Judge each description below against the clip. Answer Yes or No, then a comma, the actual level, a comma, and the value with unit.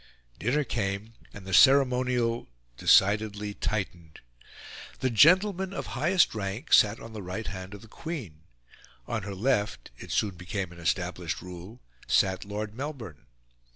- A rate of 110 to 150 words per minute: Yes, average, 140 wpm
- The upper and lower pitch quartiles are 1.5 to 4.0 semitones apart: No, average, 4.8 semitones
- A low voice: Yes, low, 105 Hz